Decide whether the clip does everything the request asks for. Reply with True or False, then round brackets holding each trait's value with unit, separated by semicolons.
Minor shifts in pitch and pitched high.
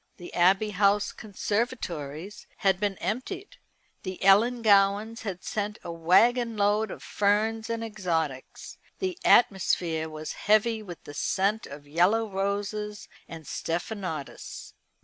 False (3.8 semitones; 200 Hz)